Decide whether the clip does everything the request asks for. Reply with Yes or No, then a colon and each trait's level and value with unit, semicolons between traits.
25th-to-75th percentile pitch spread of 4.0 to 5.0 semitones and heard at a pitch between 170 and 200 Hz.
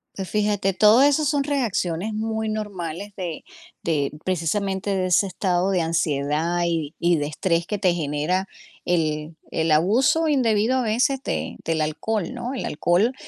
Yes: average, 4.7 semitones; medium, 185 Hz